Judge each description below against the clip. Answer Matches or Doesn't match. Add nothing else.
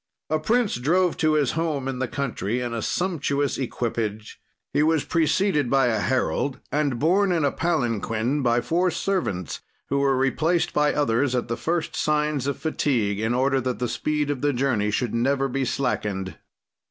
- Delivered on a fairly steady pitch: Doesn't match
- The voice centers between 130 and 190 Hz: Matches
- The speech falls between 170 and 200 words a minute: Matches